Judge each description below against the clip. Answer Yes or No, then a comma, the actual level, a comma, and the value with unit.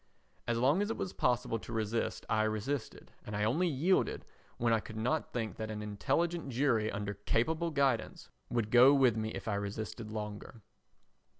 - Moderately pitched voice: No, low, 115 Hz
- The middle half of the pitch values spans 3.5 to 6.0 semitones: Yes, average, 4.2 semitones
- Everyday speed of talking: Yes, average, 175 wpm